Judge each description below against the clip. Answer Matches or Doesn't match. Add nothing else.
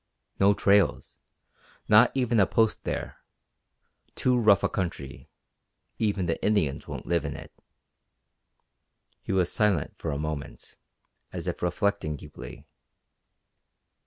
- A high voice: Doesn't match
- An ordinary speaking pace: Doesn't match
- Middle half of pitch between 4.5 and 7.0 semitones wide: Matches